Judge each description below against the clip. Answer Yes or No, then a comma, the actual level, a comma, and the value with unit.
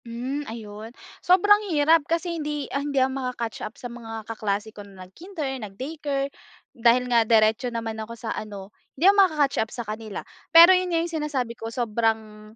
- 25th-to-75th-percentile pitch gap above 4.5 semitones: Yes, average, 5.2 semitones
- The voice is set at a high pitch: Yes, high, 240 Hz